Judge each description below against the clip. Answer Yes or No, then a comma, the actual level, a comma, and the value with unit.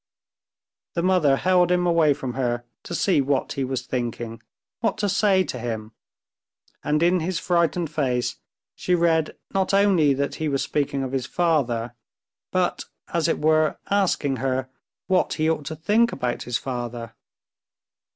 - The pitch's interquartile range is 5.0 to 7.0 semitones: Yes, wide, 5.5 semitones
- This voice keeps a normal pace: Yes, average, 160 wpm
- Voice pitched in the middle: Yes, medium, 150 Hz